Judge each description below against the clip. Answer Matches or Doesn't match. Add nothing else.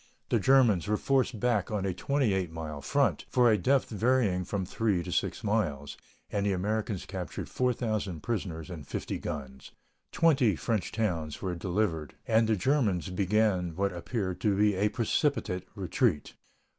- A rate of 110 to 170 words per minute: Matches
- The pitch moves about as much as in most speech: Matches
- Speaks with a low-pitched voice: Matches